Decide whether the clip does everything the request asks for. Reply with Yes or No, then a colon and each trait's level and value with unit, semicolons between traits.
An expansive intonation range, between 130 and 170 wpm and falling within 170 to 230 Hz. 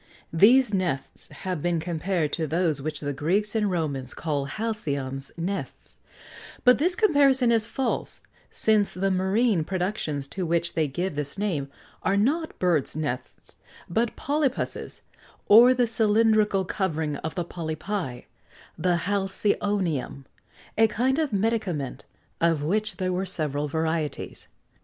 Yes: wide, 5.7 semitones; slow, 135 wpm; medium, 185 Hz